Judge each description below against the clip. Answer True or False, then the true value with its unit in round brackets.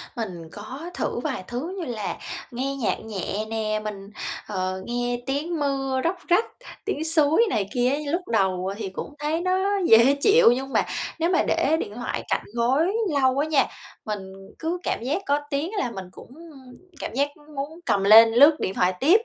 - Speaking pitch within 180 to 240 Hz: False (260 Hz)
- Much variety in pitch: True (6.7 semitones)